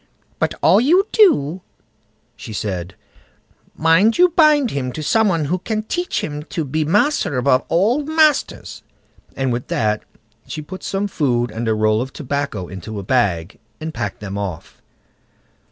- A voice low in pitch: No, medium, 145 Hz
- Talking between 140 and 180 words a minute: Yes, average, 160 wpm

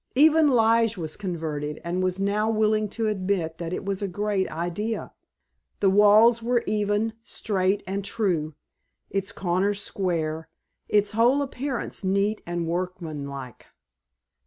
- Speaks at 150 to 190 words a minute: No, slow, 135 wpm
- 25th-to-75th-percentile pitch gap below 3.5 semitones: No, average, 3.8 semitones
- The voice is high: Yes, high, 200 Hz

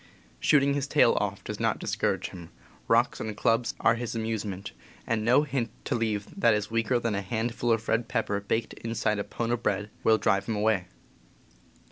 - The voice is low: Yes, low, 115 Hz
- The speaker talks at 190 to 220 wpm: Yes, average, 200 wpm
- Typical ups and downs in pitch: No, narrow, 2.1 semitones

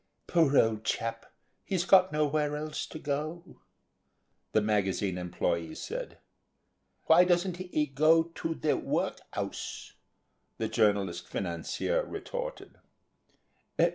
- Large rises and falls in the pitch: Yes, wide, 8.2 semitones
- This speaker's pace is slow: Yes, slow, 110 wpm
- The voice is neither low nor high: Yes, medium, 150 Hz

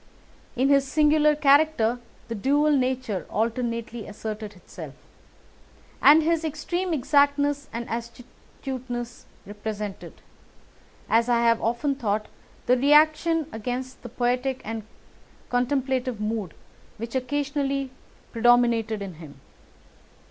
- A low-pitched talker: No, very high, 250 Hz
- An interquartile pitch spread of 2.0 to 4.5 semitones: Yes, average, 4.0 semitones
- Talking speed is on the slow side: Yes, slow, 105 wpm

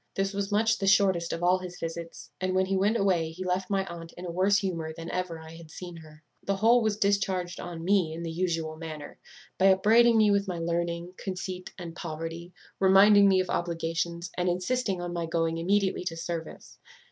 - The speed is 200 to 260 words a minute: Yes, fast, 205 wpm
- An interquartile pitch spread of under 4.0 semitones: Yes, average, 2.7 semitones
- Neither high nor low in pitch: Yes, medium, 180 Hz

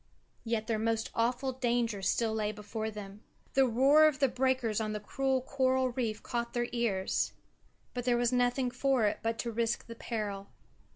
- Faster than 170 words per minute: Yes, average, 180 wpm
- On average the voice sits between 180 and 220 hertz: No, high, 235 Hz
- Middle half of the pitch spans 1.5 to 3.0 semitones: Yes, average, 2.7 semitones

